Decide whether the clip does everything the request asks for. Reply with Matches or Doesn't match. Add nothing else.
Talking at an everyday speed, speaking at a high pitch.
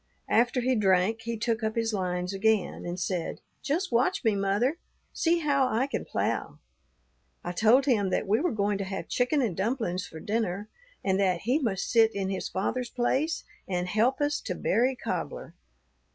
Matches